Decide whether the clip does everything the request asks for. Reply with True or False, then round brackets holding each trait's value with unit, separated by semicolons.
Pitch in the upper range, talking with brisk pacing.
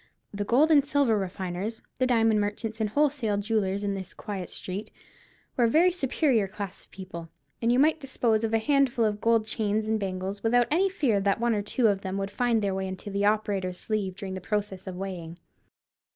True (210 Hz; 210 wpm)